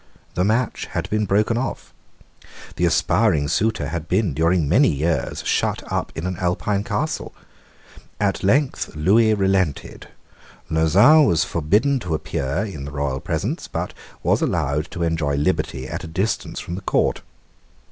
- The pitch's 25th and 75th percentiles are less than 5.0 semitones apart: No, wide, 5.4 semitones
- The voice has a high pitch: No, very low, 90 Hz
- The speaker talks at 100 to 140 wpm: No, average, 150 wpm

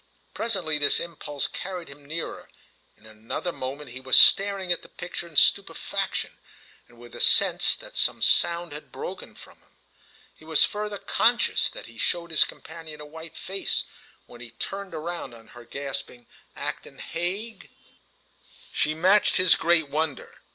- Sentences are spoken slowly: No, average, 160 wpm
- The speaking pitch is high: No, medium, 160 Hz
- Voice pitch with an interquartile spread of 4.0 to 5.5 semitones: Yes, average, 4.4 semitones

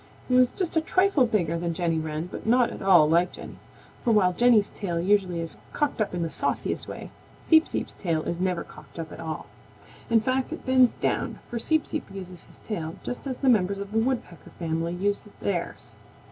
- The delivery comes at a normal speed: No, fast, 210 wpm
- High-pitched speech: Yes, high, 195 Hz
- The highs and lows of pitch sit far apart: Yes, wide, 6.4 semitones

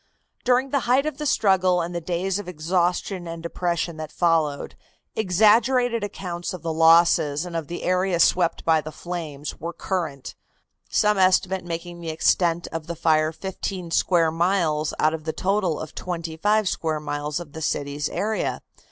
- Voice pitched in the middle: Yes, medium, 170 Hz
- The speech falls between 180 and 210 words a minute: No, average, 170 wpm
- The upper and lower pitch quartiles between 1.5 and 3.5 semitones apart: Yes, average, 3.0 semitones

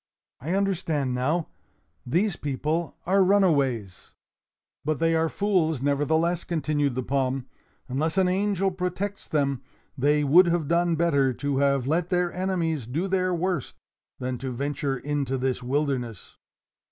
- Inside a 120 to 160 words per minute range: Yes, average, 140 wpm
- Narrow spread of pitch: No, average, 4.7 semitones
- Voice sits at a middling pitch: Yes, medium, 155 Hz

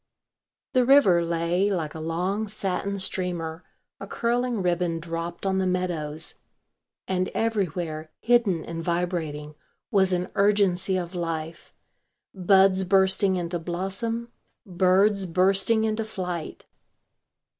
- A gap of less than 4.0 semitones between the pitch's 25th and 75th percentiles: Yes, average, 2.7 semitones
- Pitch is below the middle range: No, medium, 185 Hz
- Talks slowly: Yes, slow, 115 wpm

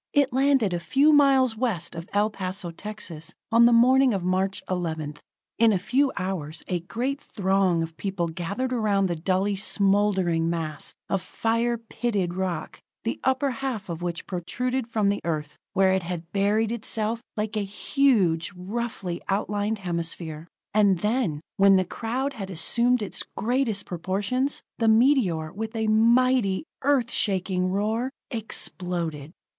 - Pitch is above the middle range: Yes, high, 200 Hz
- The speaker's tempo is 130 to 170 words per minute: Yes, average, 150 wpm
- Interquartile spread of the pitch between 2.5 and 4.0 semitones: No, average, 4.8 semitones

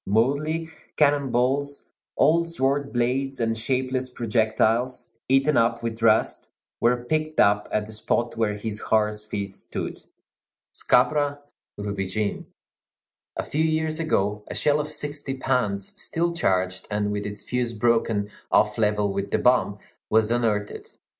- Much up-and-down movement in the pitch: No, average, 5.0 semitones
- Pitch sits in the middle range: No, low, 120 Hz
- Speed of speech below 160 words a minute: Yes, average, 140 wpm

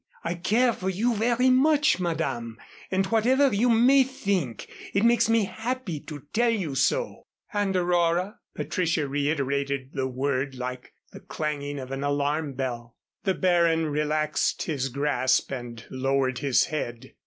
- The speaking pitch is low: No, medium, 160 Hz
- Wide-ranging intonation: Yes, wide, 7.6 semitones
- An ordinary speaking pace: Yes, average, 145 wpm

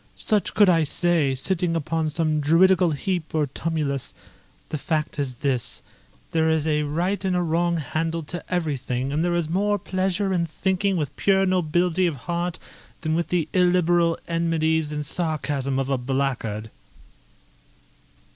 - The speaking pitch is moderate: Yes, medium, 165 Hz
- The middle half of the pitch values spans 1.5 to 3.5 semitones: Yes, average, 3.1 semitones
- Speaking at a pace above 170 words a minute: No, average, 150 wpm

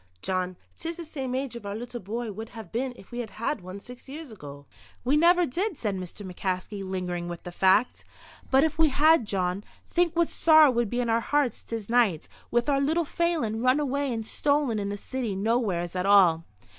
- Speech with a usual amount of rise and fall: No, wide, 6.5 semitones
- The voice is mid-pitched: No, high, 235 Hz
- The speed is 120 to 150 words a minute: No, fast, 205 wpm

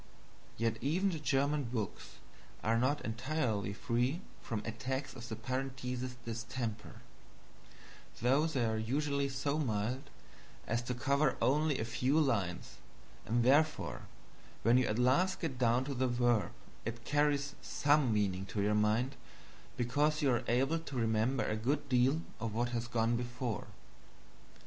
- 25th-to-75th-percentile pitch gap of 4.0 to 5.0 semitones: No, average, 3.6 semitones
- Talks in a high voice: No, low, 125 Hz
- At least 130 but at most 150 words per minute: Yes, average, 145 wpm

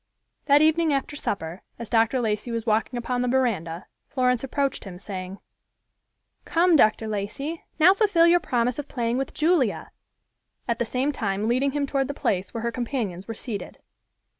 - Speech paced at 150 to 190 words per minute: Yes, average, 170 wpm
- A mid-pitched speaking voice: No, high, 245 Hz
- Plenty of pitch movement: No, average, 4.7 semitones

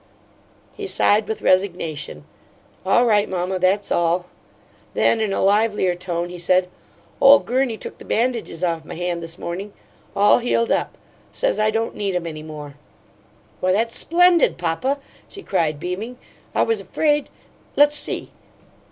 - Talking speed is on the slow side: No, average, 150 wpm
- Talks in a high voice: Yes, high, 195 Hz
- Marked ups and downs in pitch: No, average, 5.0 semitones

